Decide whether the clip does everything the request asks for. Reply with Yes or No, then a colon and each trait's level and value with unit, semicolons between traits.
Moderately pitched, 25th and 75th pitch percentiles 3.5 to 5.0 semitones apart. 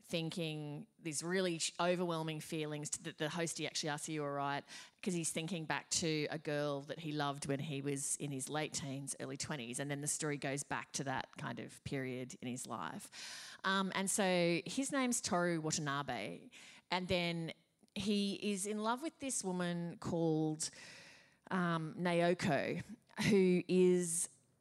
Yes: medium, 165 Hz; average, 3.9 semitones